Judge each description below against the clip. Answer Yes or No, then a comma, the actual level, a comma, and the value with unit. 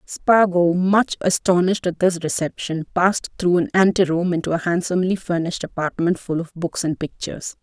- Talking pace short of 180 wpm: Yes, average, 165 wpm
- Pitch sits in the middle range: Yes, medium, 175 Hz